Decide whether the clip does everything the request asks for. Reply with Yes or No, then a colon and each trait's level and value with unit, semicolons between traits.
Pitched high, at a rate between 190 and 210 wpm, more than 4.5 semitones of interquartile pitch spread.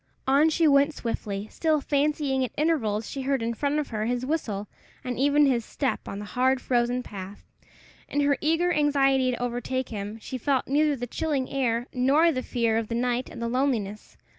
No: very high, 260 Hz; average, 195 wpm; average, 3.6 semitones